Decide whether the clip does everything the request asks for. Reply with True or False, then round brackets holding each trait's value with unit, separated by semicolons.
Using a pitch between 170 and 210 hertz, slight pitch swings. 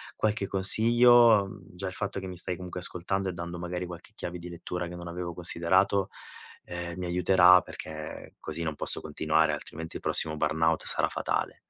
False (90 Hz; 2.0 semitones)